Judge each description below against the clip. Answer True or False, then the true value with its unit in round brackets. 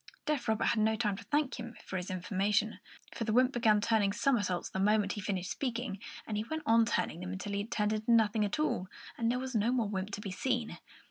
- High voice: True (215 Hz)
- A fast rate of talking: True (245 wpm)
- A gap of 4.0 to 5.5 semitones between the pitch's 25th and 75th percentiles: False (2.8 semitones)